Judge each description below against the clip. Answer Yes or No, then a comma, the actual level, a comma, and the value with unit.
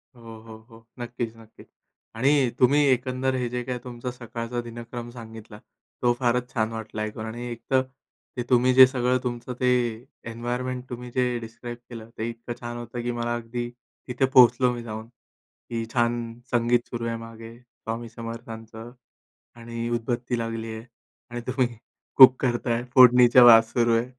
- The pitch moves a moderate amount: No, narrow, 1.4 semitones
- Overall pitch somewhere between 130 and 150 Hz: No, low, 120 Hz